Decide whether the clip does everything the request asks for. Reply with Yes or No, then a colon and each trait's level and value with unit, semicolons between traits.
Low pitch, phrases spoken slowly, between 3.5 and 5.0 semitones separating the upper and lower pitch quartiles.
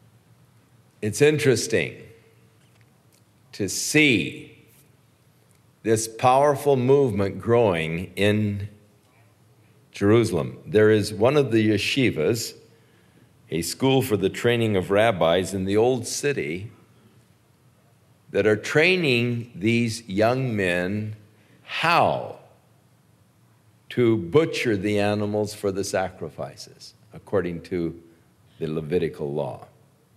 Yes: low, 110 Hz; slow, 90 wpm; average, 3.9 semitones